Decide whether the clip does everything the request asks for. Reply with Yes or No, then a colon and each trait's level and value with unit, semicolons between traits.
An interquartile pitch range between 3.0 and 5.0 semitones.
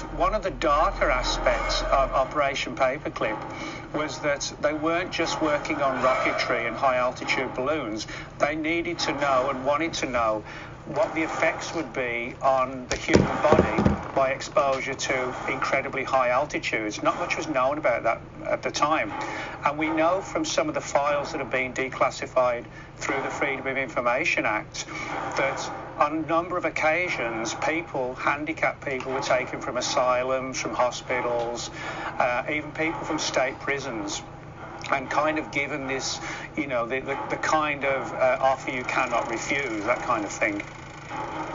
Yes: average, 3.3 semitones